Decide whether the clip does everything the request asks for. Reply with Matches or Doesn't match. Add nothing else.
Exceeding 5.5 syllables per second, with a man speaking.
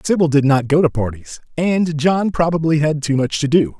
Doesn't match